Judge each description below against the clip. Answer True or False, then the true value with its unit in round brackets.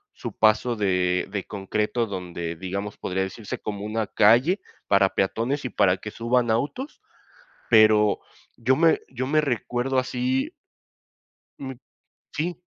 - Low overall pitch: True (110 Hz)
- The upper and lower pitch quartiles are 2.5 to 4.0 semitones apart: False (4.6 semitones)